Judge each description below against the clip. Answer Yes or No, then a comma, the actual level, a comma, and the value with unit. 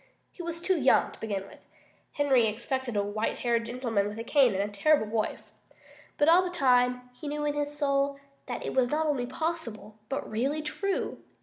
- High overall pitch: Yes, very high, 260 Hz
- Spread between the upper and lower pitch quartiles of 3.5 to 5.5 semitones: Yes, average, 4.7 semitones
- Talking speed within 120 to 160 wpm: No, average, 200 wpm